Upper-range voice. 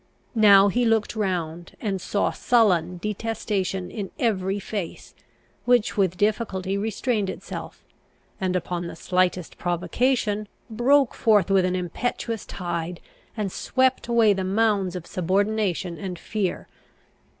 Yes: high, 195 Hz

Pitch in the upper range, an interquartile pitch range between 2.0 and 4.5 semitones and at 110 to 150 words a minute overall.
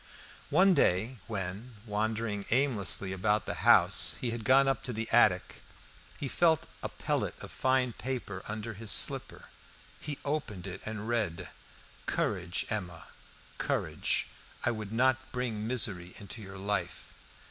No: low, 110 Hz; average, 4.2 semitones; average, 140 wpm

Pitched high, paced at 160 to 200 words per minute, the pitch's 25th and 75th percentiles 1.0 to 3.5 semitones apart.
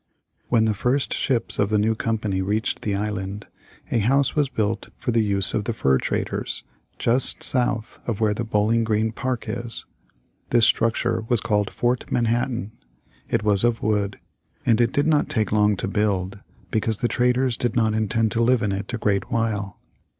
No: low, 110 Hz; average, 180 wpm; narrow, 2.4 semitones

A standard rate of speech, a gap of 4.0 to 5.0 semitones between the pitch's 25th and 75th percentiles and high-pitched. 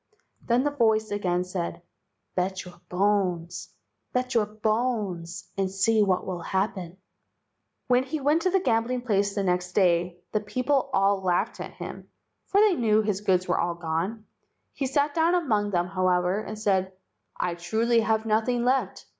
Yes: average, 165 wpm; average, 4.7 semitones; high, 205 Hz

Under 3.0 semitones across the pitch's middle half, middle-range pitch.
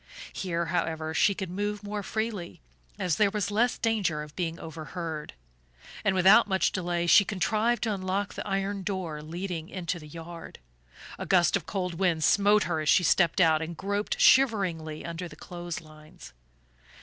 No: average, 3.6 semitones; medium, 180 Hz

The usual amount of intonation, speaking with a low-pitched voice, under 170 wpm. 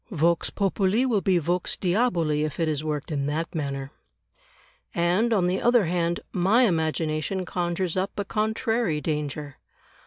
No: average, 4.2 semitones; medium, 175 Hz; average, 150 wpm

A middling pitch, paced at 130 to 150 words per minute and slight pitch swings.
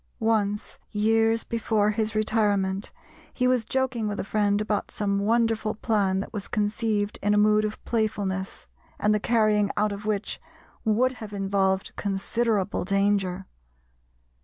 No: high, 210 Hz; average, 140 wpm; narrow, 1.7 semitones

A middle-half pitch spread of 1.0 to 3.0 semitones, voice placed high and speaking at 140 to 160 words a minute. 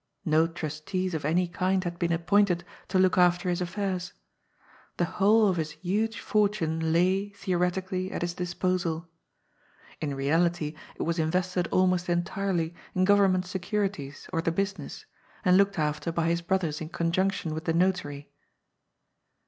No: narrow, 2.4 semitones; medium, 180 Hz; average, 150 wpm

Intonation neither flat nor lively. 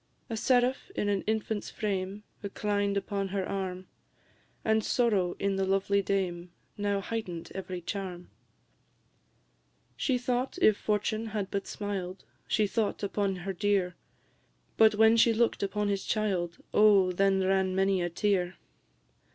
No: narrow, 2.1 semitones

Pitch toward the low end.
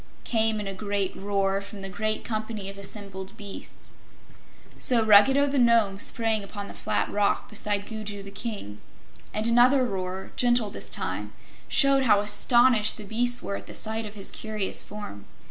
No: high, 210 Hz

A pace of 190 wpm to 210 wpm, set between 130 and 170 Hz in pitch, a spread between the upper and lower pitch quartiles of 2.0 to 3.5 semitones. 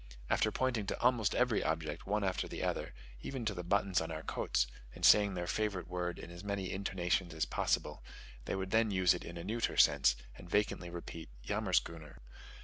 No: average, 195 wpm; very low, 95 Hz; average, 3.2 semitones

